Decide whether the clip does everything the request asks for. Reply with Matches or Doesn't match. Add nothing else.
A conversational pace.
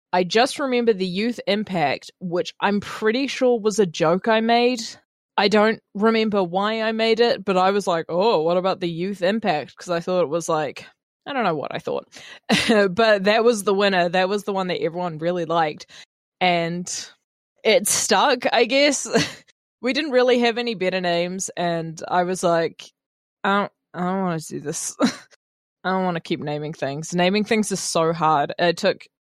Matches